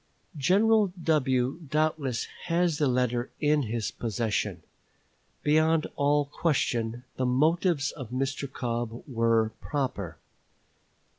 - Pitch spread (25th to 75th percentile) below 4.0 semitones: No, average, 4.5 semitones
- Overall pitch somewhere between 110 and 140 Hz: Yes, low, 135 Hz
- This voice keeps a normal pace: No, slow, 100 wpm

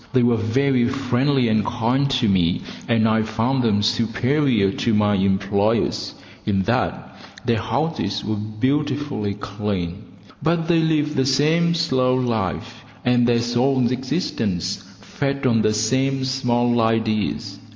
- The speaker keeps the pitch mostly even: No, average, 3.9 semitones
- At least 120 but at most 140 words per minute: Yes, slow, 135 wpm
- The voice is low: Yes, low, 120 Hz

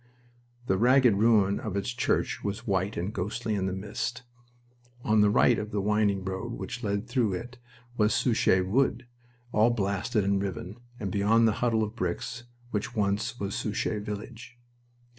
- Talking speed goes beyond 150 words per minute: Yes, average, 165 wpm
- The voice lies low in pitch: Yes, low, 105 Hz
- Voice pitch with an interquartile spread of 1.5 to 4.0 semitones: Yes, average, 2.8 semitones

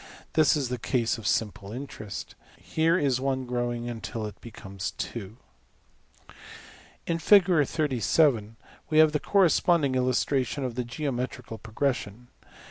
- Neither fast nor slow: No, slow, 115 wpm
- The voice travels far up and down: No, average, 4.7 semitones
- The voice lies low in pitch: Yes, low, 125 Hz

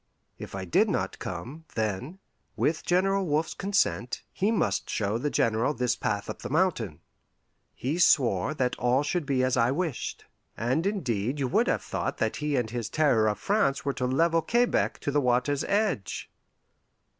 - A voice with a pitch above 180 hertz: No, low, 135 Hz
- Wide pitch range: Yes, wide, 5.8 semitones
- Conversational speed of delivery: Yes, average, 175 wpm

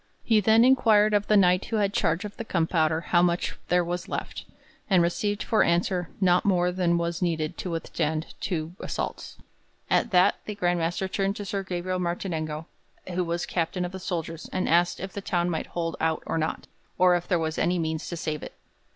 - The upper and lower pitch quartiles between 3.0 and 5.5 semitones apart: No, narrow, 2.5 semitones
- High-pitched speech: No, medium, 175 Hz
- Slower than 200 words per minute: No, fast, 205 wpm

